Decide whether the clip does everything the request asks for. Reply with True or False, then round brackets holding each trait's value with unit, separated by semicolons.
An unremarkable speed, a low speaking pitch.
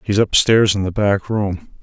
True (195 wpm; 100 Hz)